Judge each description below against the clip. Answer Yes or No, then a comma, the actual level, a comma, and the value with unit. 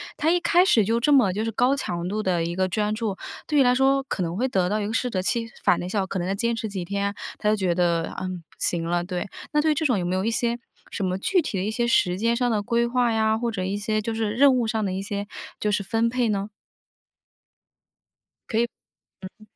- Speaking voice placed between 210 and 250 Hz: Yes, high, 215 Hz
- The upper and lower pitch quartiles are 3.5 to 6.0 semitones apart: Yes, average, 4.0 semitones